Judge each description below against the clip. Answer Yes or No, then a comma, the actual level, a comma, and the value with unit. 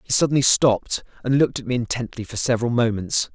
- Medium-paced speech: Yes, average, 195 wpm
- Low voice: Yes, low, 120 Hz